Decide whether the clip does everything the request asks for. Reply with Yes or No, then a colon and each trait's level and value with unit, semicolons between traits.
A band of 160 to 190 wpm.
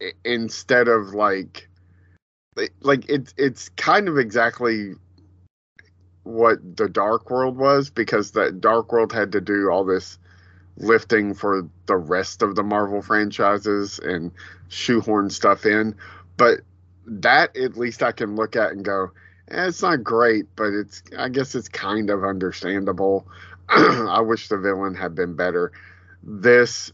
No: average, 145 wpm